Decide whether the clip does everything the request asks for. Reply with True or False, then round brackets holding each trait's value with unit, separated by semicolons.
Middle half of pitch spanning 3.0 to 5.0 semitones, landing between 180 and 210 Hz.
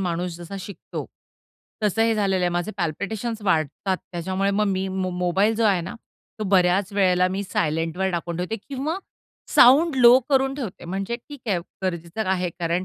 True (3.7 semitones; 190 Hz)